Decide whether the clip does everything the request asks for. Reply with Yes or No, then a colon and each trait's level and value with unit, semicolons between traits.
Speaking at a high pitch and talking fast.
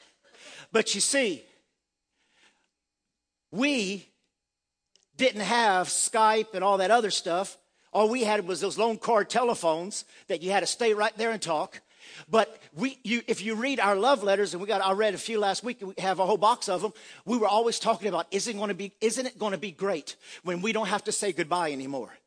Yes: high, 210 Hz; fast, 210 wpm